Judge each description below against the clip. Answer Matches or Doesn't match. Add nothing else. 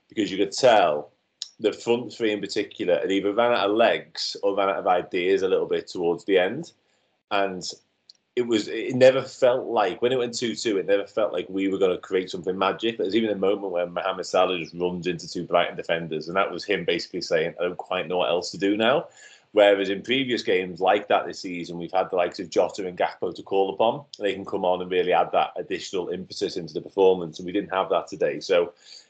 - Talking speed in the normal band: Doesn't match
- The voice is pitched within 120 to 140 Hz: Doesn't match